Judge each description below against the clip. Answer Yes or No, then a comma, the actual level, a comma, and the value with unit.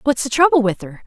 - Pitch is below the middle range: No, very high, 250 Hz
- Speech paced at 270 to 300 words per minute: Yes, fast, 285 wpm